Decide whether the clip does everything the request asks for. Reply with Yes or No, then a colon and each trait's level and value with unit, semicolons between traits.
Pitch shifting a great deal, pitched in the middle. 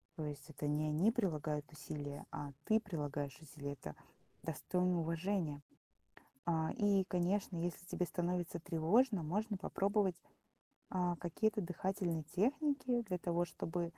No: average, 4.3 semitones; medium, 175 Hz